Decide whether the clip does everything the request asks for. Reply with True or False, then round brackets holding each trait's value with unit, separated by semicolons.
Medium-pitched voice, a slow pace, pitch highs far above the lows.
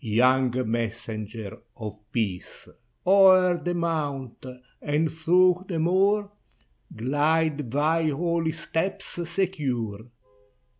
True (155 Hz; 90 wpm; 6.6 semitones)